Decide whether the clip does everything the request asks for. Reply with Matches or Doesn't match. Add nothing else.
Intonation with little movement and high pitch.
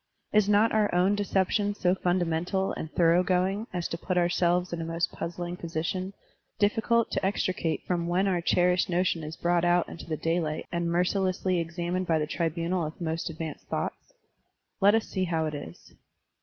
Doesn't match